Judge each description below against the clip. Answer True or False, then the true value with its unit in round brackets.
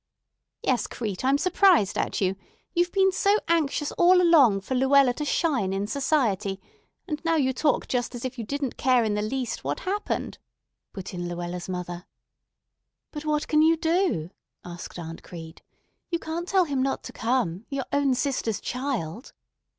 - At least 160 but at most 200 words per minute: True (165 wpm)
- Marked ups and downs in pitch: True (7.7 semitones)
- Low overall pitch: False (260 Hz)